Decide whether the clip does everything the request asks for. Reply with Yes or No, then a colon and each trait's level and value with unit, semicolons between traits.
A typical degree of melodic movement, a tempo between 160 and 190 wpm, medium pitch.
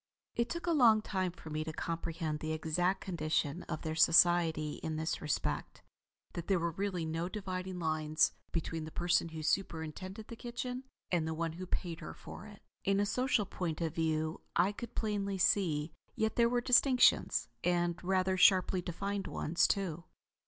Yes: average, 3.7 semitones; average, 175 wpm; medium, 175 Hz